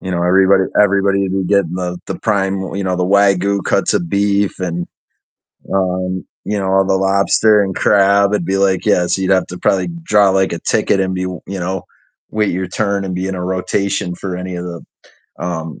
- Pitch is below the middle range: Yes, very low, 95 Hz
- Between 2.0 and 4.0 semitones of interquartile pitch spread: No, narrow, 1.5 semitones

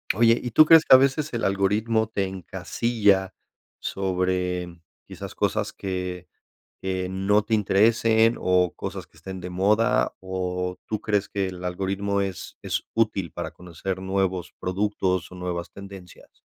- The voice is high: No, very low, 95 Hz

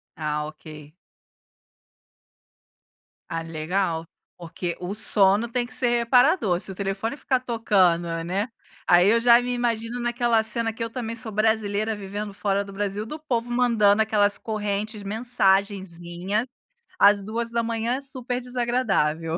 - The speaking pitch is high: Yes, high, 215 Hz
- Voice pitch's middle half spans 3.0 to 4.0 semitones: Yes, average, 3.5 semitones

